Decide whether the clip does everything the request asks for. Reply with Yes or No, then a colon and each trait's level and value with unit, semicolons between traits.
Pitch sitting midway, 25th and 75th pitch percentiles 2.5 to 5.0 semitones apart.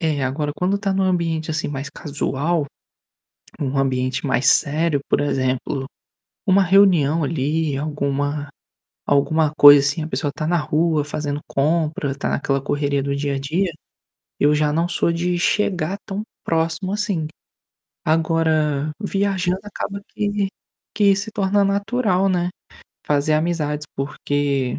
Yes: medium, 155 Hz; average, 4.1 semitones